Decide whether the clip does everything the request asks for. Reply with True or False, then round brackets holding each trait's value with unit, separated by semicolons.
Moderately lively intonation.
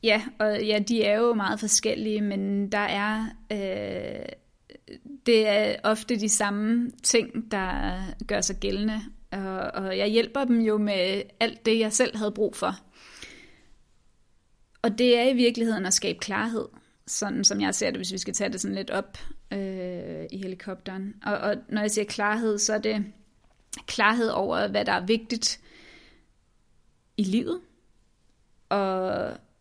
False (2.1 semitones)